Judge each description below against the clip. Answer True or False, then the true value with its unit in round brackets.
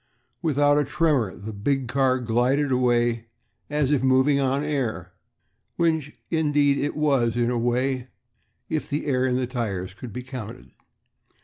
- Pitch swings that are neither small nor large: True (3.3 semitones)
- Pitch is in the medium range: False (130 Hz)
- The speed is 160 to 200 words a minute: False (150 wpm)